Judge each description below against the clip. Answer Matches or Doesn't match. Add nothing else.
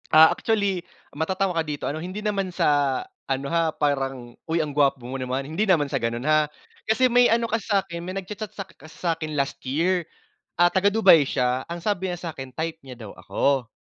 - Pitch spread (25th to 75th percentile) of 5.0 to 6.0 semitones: Matches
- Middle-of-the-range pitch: Matches